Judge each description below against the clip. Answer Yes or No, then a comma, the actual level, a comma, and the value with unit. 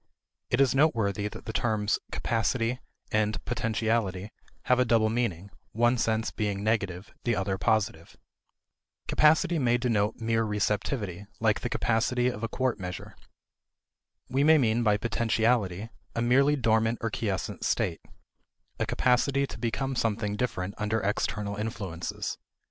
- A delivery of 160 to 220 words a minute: No, slow, 135 wpm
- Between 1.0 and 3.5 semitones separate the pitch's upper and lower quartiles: Yes, average, 2.8 semitones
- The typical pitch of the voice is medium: No, low, 110 Hz